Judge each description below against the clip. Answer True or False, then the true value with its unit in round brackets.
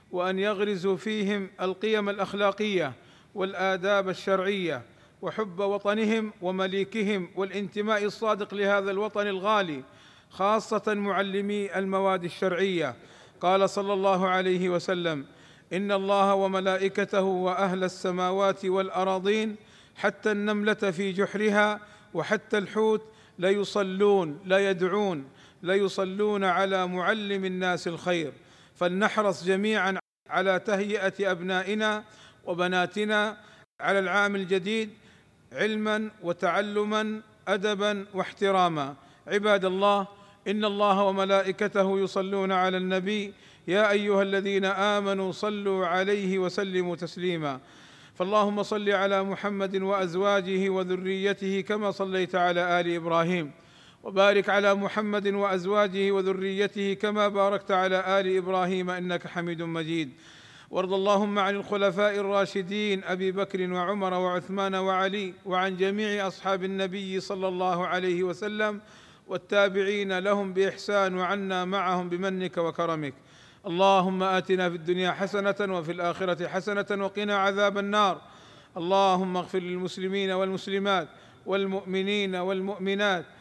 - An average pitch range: False (1.7 semitones)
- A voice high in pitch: True (195 Hz)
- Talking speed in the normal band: True (100 wpm)